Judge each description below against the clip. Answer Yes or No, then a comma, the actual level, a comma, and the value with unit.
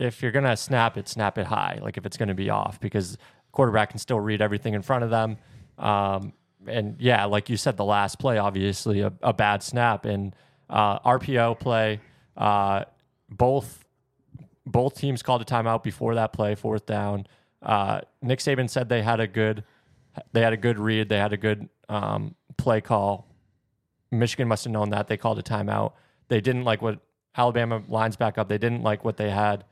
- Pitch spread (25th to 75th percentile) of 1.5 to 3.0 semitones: Yes, narrow, 2.6 semitones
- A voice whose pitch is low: Yes, low, 110 Hz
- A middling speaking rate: Yes, average, 195 wpm